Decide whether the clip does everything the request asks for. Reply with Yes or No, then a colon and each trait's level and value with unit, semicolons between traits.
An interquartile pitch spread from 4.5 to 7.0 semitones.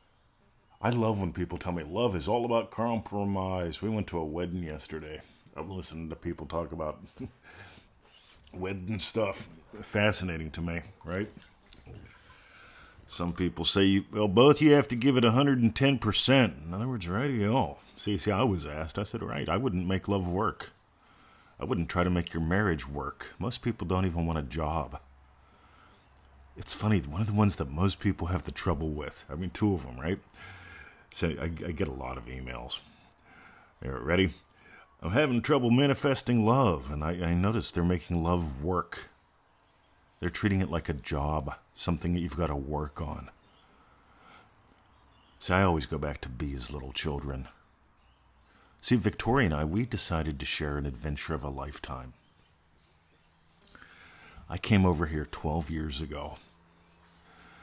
Yes: average, 4.8 semitones